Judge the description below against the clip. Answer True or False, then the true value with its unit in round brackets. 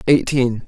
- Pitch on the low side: True (130 Hz)